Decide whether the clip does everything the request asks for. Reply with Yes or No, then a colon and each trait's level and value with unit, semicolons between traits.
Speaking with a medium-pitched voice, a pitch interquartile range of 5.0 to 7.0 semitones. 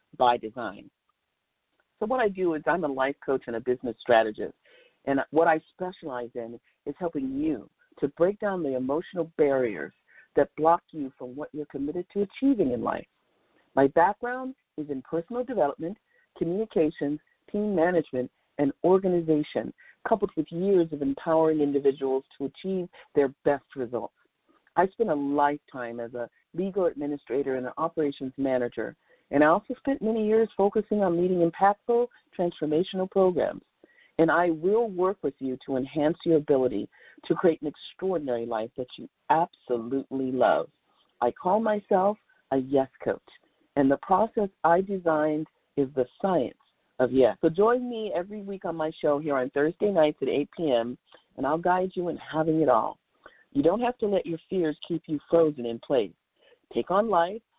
Yes: medium, 160 Hz; wide, 5.6 semitones